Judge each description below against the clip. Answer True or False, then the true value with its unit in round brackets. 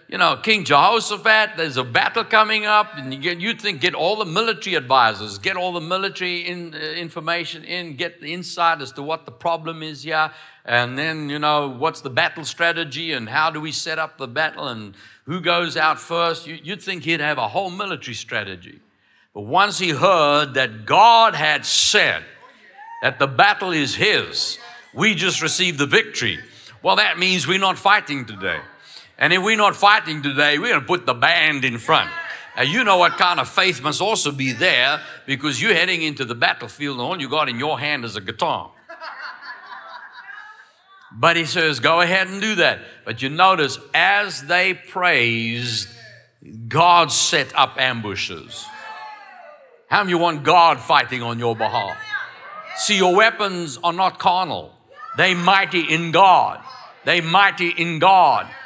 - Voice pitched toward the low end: False (170 Hz)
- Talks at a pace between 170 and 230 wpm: True (175 wpm)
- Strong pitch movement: False (4.4 semitones)